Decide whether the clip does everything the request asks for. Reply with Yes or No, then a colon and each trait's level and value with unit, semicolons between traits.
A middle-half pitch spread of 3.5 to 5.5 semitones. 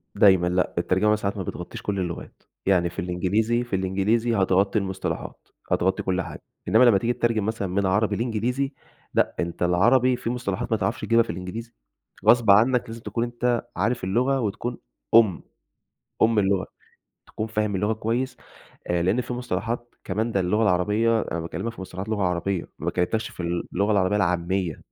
Yes: average, 3.9 semitones